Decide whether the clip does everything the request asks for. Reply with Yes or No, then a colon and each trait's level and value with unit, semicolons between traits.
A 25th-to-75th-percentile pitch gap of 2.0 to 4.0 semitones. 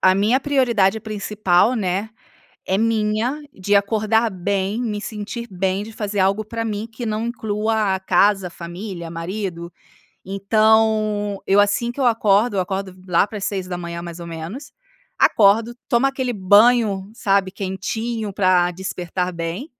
Yes: average, 2.8 semitones